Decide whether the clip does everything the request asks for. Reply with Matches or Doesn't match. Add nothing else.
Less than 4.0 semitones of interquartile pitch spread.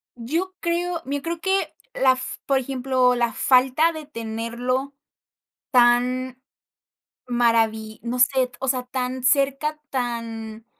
Matches